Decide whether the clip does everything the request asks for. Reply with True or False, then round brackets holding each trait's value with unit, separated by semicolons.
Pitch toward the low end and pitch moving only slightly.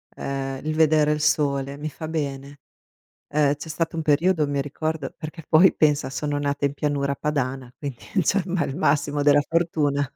False (145 Hz; 1.9 semitones)